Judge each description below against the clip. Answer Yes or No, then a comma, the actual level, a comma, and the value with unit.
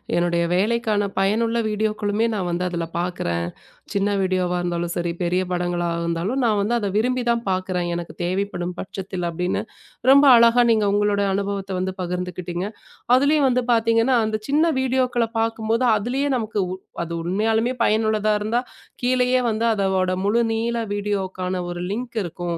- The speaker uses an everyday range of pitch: Yes, average, 4.2 semitones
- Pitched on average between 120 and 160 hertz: No, high, 205 Hz